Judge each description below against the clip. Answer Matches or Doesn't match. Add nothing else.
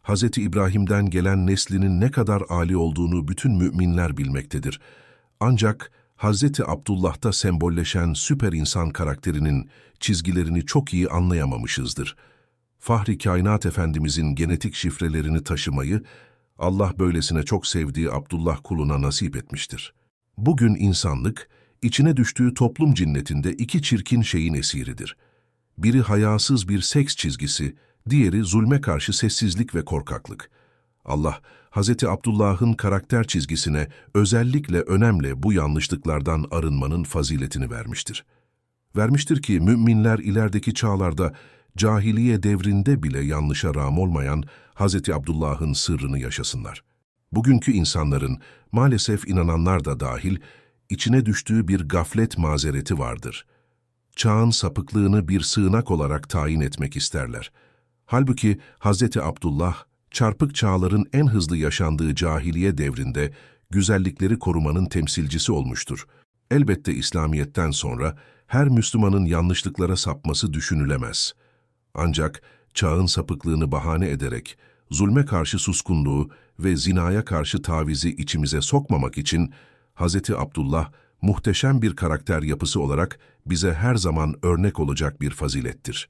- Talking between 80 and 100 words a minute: Doesn't match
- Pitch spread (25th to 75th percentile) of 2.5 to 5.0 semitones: Doesn't match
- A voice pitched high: Doesn't match